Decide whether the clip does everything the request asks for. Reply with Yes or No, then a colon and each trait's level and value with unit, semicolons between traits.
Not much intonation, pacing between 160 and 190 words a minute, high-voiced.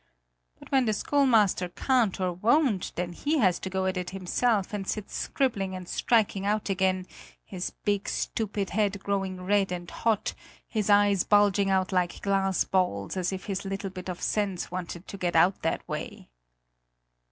Yes: narrow, 2.0 semitones; average, 175 wpm; high, 195 Hz